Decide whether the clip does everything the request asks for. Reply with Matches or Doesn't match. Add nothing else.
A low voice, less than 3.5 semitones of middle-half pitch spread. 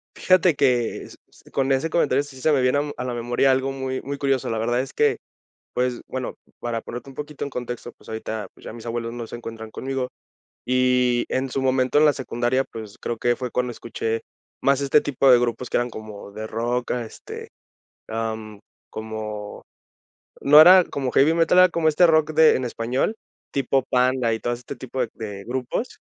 Matches